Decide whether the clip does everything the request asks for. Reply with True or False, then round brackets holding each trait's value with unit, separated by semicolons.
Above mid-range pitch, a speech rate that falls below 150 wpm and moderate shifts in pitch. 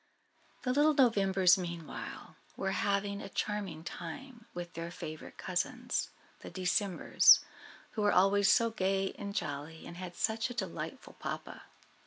True (195 Hz; 140 wpm; 3.9 semitones)